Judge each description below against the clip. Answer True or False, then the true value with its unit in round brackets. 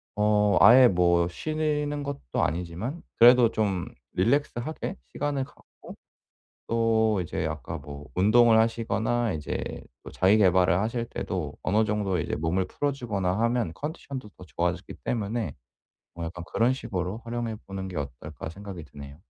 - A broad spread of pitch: False (5.0 semitones)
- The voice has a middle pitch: False (105 Hz)